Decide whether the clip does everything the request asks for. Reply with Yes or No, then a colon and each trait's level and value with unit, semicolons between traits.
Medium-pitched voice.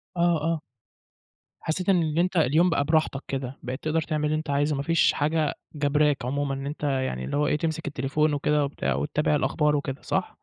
Yes: medium, 150 Hz